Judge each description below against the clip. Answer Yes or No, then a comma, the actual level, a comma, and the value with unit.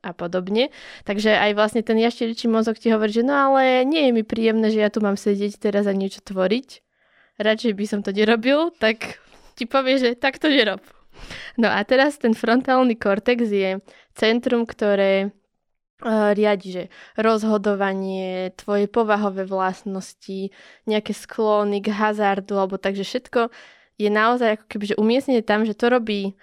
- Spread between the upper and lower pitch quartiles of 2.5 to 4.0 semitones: Yes, average, 2.9 semitones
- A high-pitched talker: Yes, high, 215 Hz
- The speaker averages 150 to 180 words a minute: Yes, average, 160 wpm